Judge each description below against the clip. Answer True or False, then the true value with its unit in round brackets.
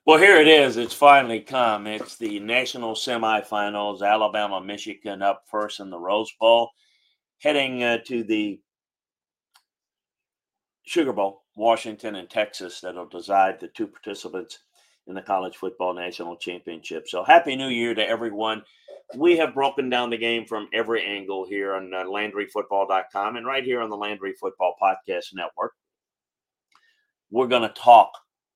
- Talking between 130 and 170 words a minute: True (145 wpm)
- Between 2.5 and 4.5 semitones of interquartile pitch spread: True (3.6 semitones)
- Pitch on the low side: True (110 Hz)